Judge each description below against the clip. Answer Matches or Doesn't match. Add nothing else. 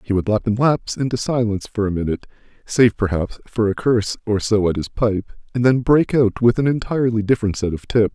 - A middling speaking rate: Doesn't match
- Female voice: Doesn't match